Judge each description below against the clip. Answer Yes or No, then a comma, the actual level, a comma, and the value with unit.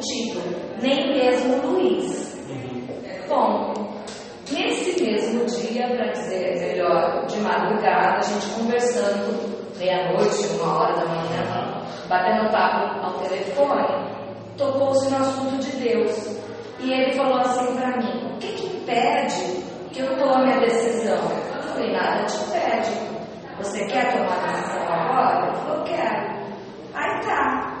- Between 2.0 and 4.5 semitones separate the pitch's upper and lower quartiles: Yes, average, 3.3 semitones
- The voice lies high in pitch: Yes, high, 245 Hz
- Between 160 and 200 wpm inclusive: No, average, 140 wpm